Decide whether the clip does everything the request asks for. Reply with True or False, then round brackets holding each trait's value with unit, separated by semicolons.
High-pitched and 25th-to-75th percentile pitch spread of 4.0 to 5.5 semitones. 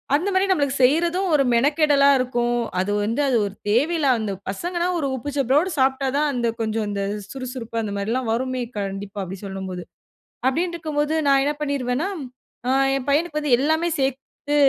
True (270 Hz; 4.7 semitones)